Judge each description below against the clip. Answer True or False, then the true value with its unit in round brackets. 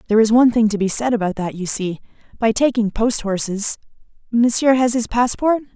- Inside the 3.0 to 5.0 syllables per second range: False (5.7 syllables/s)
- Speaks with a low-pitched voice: False (225 Hz)